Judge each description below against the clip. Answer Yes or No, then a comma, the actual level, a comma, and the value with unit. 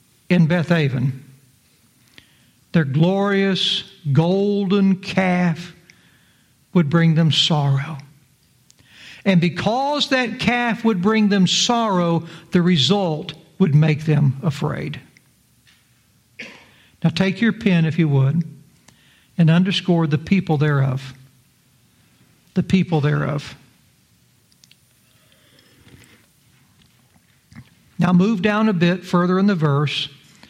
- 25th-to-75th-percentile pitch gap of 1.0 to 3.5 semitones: No, average, 4.4 semitones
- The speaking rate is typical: No, slow, 95 wpm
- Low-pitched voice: No, medium, 170 Hz